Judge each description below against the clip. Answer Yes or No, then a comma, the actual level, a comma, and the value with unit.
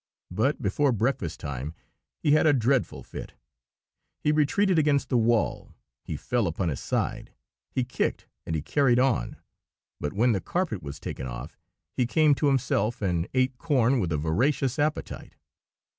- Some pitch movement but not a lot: No, wide, 8.0 semitones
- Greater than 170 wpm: No, average, 160 wpm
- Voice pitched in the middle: No, low, 125 Hz